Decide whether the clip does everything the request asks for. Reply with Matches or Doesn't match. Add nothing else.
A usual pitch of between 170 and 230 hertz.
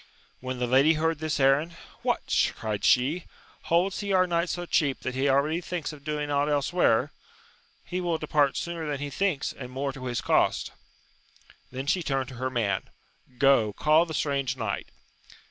Doesn't match